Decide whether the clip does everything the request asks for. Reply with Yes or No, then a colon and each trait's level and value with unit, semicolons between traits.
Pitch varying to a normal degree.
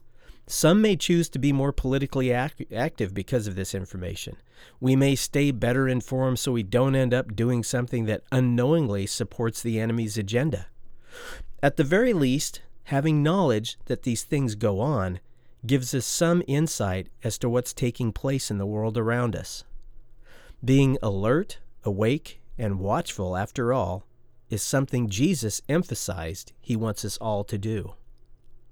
Yes: average, 3.8 semitones